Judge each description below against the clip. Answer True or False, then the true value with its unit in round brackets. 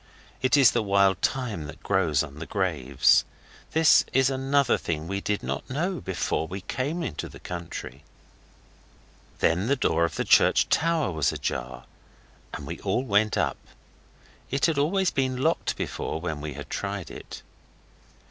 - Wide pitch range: True (8.9 semitones)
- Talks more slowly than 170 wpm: True (160 wpm)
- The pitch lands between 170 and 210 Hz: False (100 Hz)